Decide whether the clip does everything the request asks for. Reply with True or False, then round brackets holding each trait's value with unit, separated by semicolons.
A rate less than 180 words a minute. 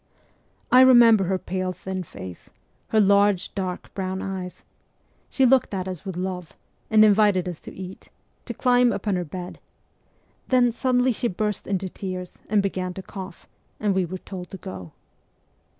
True (165 wpm)